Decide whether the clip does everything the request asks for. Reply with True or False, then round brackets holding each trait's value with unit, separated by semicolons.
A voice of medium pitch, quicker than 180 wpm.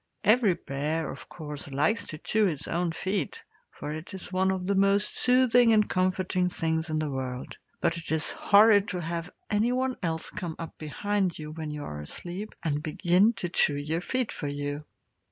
True (175 Hz; 190 wpm)